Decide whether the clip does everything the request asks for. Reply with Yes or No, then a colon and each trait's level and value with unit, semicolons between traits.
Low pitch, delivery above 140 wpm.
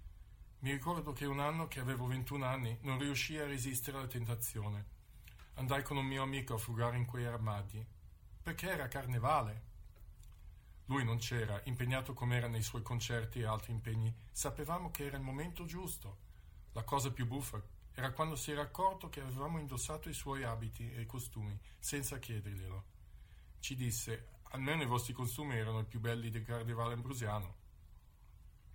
Yes: low, 120 Hz; average, 165 wpm